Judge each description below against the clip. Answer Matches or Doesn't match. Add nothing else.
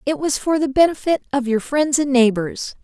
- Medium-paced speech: Doesn't match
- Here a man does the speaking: Doesn't match